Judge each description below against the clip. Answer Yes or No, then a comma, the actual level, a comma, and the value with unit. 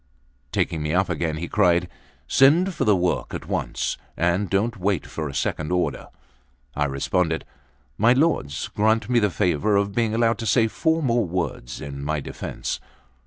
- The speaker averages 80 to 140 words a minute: No, average, 170 wpm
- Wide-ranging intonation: Yes, wide, 6.1 semitones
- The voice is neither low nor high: No, very low, 95 Hz